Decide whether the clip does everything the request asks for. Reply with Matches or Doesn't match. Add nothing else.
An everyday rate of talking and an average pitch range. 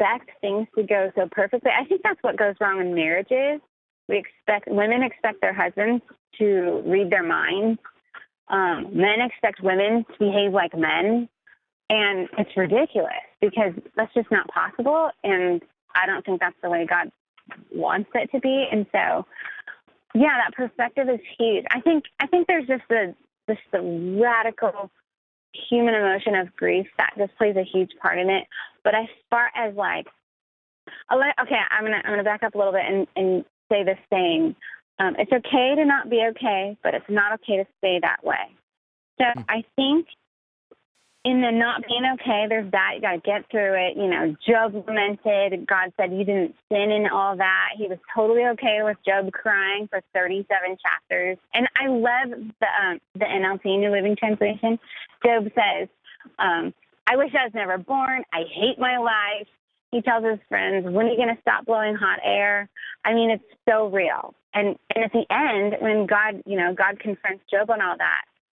Matches